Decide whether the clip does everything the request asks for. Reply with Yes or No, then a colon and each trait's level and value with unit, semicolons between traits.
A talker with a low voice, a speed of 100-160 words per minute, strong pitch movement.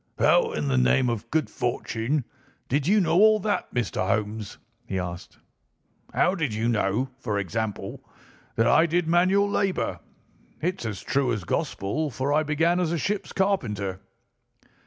Yes: low, 130 Hz; average, 155 wpm; wide, 8.3 semitones